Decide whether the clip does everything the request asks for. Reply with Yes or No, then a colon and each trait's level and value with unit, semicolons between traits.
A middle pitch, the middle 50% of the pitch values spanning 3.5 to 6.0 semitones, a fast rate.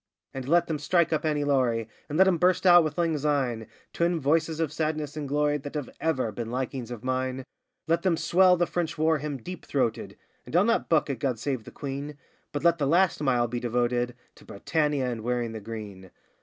Yes: medium, 145 Hz; average, 4.7 semitones; fast, 215 wpm